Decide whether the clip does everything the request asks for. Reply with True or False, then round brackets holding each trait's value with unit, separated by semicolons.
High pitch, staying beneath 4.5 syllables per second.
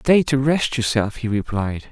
False (120 Hz; 4.3 syllables/s)